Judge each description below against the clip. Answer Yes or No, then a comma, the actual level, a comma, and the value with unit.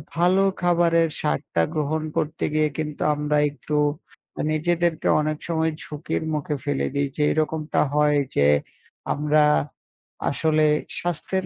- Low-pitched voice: No, medium, 155 Hz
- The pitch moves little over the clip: Yes, narrow, 1.8 semitones